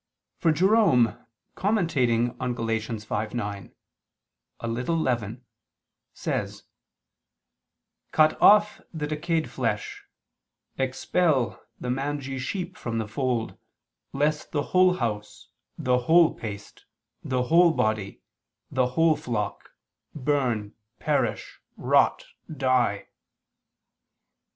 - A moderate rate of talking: No, slow, 95 wpm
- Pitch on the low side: Yes, low, 130 Hz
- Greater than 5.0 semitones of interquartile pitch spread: Yes, wide, 5.6 semitones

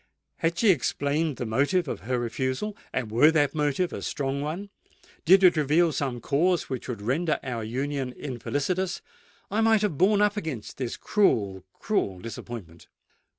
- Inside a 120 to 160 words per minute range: Yes, average, 150 wpm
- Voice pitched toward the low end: No, medium, 145 Hz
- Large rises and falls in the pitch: Yes, wide, 6.3 semitones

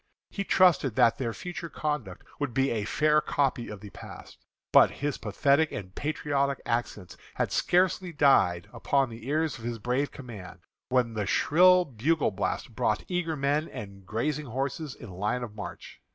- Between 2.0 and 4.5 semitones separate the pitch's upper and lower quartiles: No, wide, 5.5 semitones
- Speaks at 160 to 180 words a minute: Yes, average, 165 wpm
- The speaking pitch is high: No, low, 135 Hz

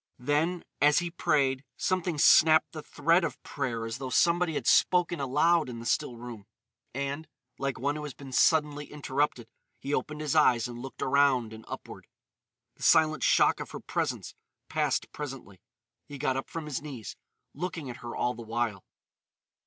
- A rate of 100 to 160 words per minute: No, average, 175 wpm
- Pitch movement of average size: Yes, average, 3.9 semitones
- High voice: No, medium, 140 Hz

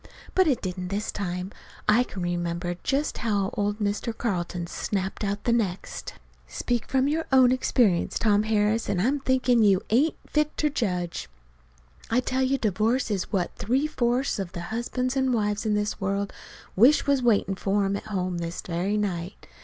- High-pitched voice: Yes, high, 210 Hz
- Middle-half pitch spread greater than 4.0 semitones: Yes, average, 4.7 semitones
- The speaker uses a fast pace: No, average, 175 wpm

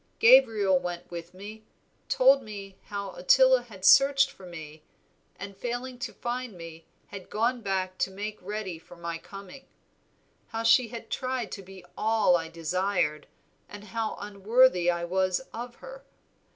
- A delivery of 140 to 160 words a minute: Yes, average, 150 wpm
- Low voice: No, high, 200 Hz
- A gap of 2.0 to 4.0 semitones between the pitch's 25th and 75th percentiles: No, average, 4.9 semitones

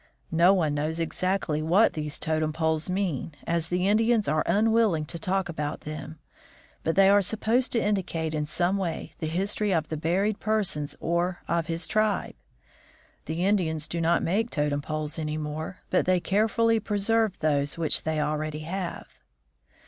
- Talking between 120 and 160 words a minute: No, average, 170 wpm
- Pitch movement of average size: Yes, average, 4.2 semitones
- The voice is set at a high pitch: No, medium, 170 Hz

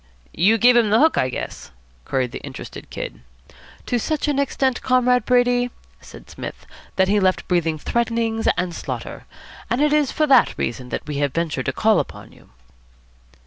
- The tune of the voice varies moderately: No, wide, 6.8 semitones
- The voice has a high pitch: Yes, high, 225 Hz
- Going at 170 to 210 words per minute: Yes, average, 180 wpm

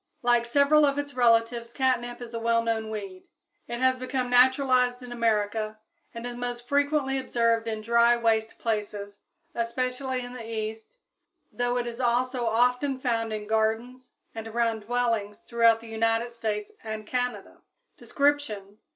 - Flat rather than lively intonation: Yes, narrow, 2.1 semitones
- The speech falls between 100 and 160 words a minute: Yes, average, 150 wpm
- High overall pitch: Yes, high, 235 Hz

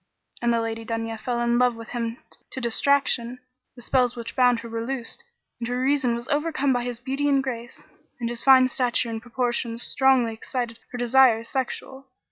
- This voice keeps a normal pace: Yes, average, 190 wpm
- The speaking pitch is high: Yes, high, 245 Hz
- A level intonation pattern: Yes, narrow, 2.1 semitones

